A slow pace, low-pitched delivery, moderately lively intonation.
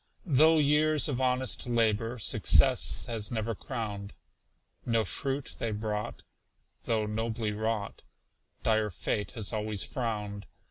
Yes: slow, 120 wpm; low, 115 Hz; average, 3.1 semitones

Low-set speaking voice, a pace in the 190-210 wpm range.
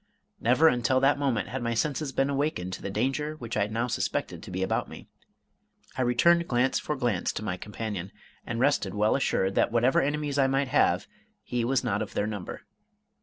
Yes: low, 125 Hz; average, 200 wpm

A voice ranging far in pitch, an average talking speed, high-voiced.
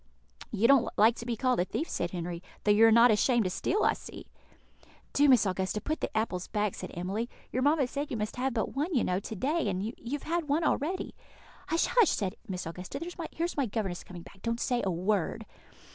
No: wide, 6.4 semitones; fast, 225 wpm; high, 225 Hz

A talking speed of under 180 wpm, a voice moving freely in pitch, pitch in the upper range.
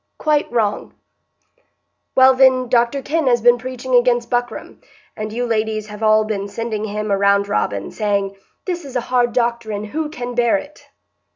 No: average, 165 wpm; average, 3.2 semitones; high, 235 Hz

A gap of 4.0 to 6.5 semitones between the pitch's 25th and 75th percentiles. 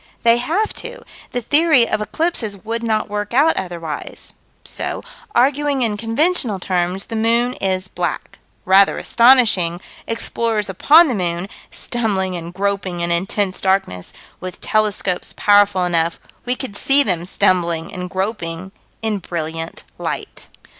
Yes: average, 4.6 semitones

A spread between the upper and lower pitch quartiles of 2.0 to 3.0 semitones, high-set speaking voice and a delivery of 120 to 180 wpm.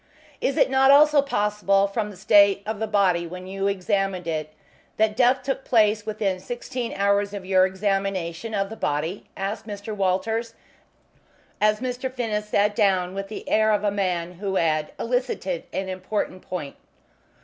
Yes: average, 2.7 semitones; high, 200 Hz; average, 165 wpm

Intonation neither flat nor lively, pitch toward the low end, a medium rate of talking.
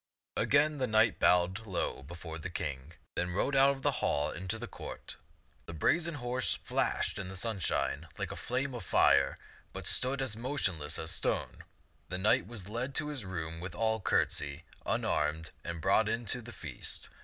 No: wide, 7.2 semitones; low, 100 Hz; average, 185 wpm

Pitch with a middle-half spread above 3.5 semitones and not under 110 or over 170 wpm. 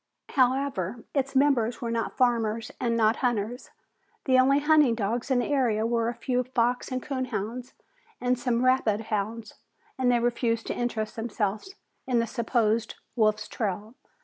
No: narrow, 2.5 semitones; average, 155 wpm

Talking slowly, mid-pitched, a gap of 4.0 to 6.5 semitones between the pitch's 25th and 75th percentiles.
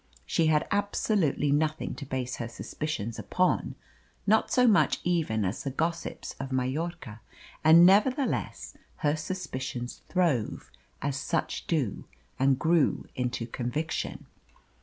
Yes: slow, 120 wpm; medium, 150 Hz; average, 5.0 semitones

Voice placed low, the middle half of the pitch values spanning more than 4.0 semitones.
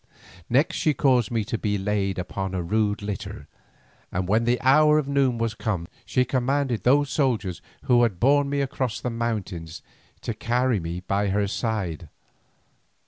Yes: low, 115 Hz; average, 4.9 semitones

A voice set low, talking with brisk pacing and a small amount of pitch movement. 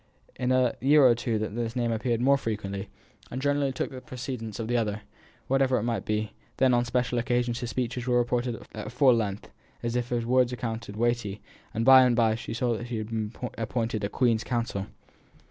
Yes: low, 120 Hz; fast, 210 wpm; narrow, 2.0 semitones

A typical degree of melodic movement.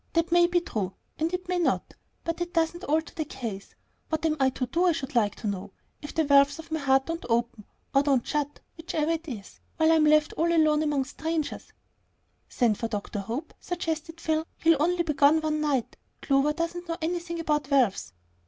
Yes: average, 3.7 semitones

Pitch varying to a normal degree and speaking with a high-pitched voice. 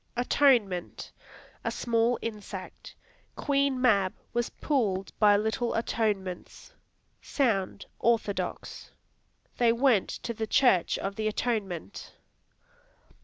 Yes: average, 3.6 semitones; high, 225 Hz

